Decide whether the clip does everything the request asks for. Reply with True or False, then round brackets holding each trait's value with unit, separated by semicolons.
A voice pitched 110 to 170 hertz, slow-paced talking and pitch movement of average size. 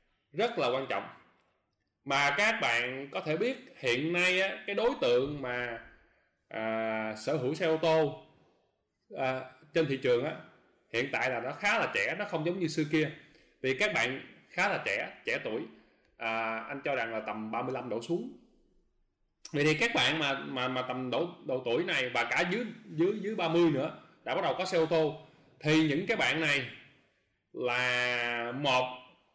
False (140 Hz; 185 wpm; 4.9 semitones)